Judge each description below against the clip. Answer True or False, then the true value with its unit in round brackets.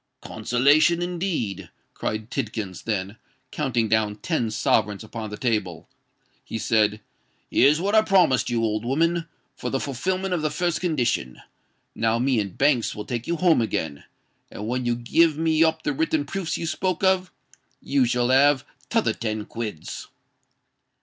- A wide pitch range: True (6.6 semitones)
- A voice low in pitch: True (125 Hz)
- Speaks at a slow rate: False (155 wpm)